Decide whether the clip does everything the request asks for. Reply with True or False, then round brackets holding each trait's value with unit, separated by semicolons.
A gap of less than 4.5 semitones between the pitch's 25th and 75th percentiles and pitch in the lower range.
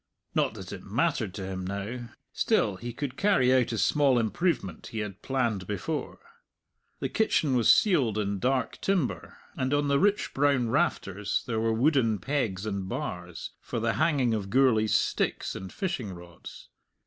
False (5.6 semitones; 115 Hz)